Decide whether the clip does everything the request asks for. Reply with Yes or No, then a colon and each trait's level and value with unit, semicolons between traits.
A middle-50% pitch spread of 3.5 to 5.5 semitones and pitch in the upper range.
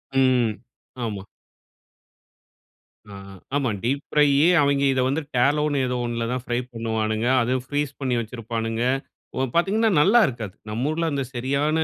No: average, 3.8 semitones; low, 130 Hz